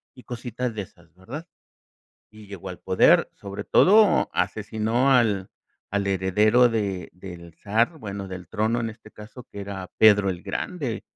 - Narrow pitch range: No, average, 3.5 semitones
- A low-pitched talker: Yes, low, 105 Hz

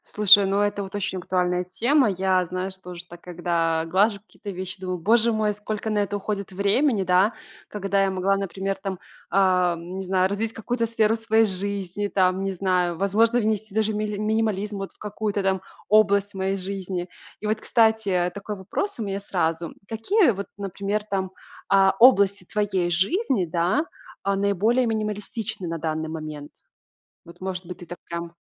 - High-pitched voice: Yes, high, 195 Hz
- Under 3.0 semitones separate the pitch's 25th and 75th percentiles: Yes, narrow, 2.6 semitones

